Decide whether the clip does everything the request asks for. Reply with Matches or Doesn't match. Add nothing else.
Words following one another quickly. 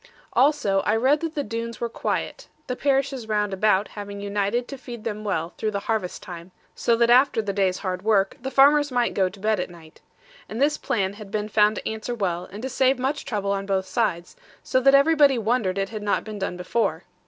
Matches